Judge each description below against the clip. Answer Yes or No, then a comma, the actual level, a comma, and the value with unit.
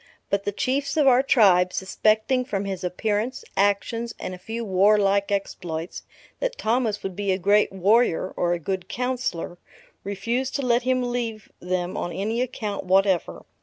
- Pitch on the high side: Yes, high, 205 Hz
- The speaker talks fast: No, average, 165 wpm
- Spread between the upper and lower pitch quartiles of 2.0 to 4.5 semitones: Yes, average, 4.2 semitones